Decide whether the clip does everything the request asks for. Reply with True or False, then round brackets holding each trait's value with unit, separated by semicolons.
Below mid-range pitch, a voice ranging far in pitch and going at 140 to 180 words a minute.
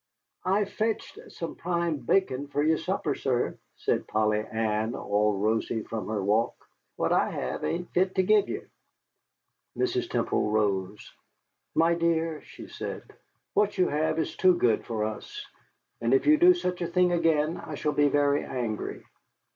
False (155 Hz; 8.4 semitones; 165 wpm)